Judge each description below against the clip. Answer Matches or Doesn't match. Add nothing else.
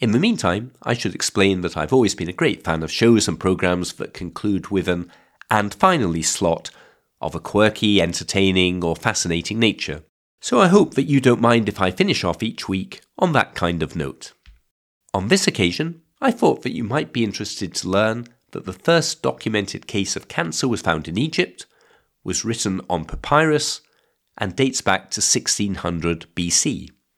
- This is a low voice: Matches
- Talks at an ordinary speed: Matches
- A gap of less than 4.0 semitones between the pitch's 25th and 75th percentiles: Doesn't match